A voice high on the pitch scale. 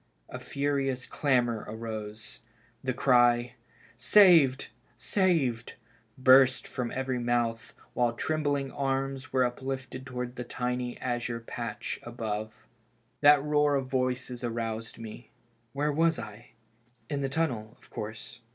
No: low, 125 Hz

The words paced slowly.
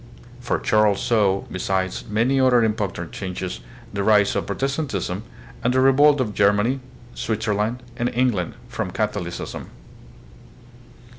Yes: slow, 120 wpm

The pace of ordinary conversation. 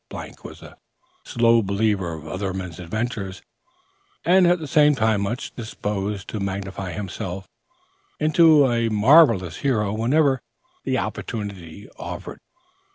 No: slow, 120 wpm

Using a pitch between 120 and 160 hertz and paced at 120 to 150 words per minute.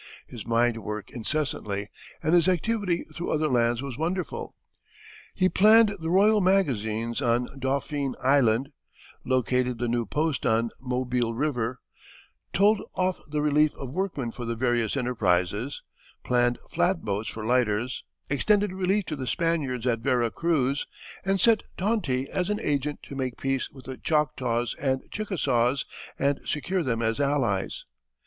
Yes: low, 135 Hz; average, 145 wpm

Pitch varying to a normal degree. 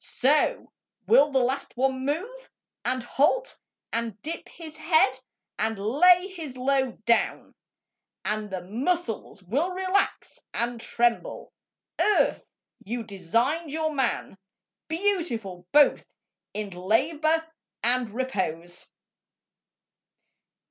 No: wide, 6.2 semitones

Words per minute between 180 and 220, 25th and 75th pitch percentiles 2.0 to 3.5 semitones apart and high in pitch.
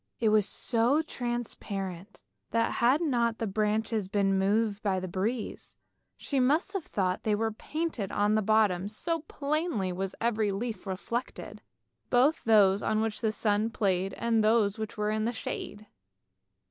No: average, 160 wpm; average, 2.9 semitones; high, 215 Hz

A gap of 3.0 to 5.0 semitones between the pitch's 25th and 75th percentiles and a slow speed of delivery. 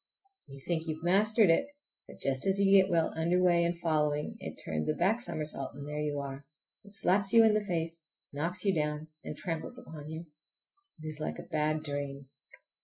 No: average, 4.0 semitones; fast, 205 wpm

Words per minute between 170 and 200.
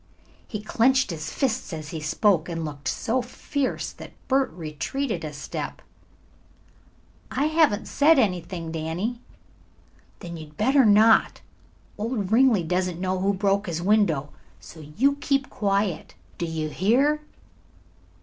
No: slow, 135 wpm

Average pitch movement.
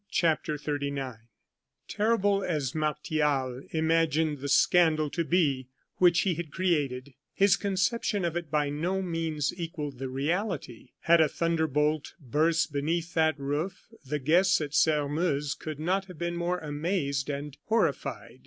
Yes: average, 3.1 semitones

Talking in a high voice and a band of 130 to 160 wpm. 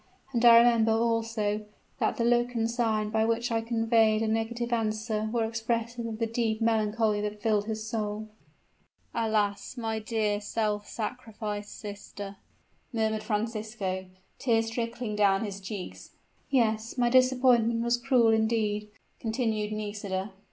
Yes: high, 225 Hz; average, 140 wpm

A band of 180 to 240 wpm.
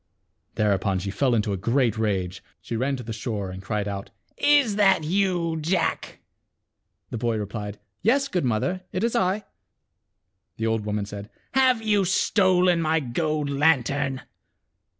No: average, 165 wpm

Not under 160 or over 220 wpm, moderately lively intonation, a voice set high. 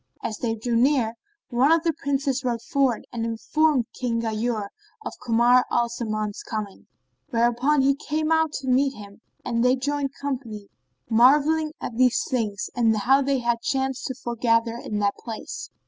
Yes: average, 165 wpm; average, 3.2 semitones; high, 245 Hz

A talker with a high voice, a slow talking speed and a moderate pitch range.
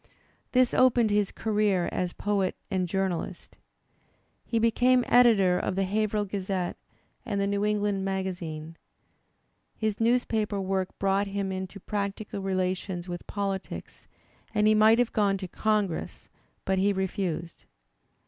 No: high, 200 Hz; slow, 130 wpm; narrow, 2.1 semitones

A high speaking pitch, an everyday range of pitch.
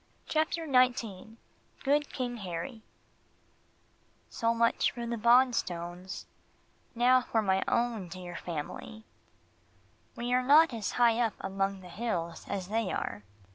Yes: high, 230 Hz; average, 4.6 semitones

